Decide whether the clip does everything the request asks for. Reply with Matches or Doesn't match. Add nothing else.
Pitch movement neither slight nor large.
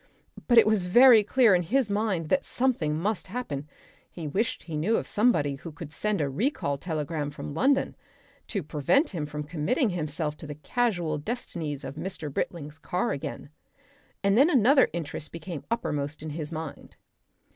Doesn't match